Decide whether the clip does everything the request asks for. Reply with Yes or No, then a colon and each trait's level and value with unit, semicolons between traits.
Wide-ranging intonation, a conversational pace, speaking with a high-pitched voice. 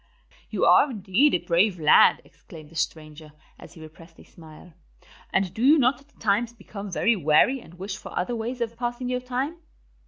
Yes: wide, 6.9 semitones; average, 190 wpm; high, 205 Hz